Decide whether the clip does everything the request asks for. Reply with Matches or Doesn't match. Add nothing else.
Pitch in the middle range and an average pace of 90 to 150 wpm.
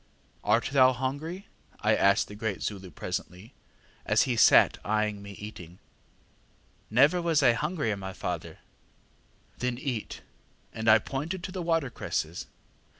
Doesn't match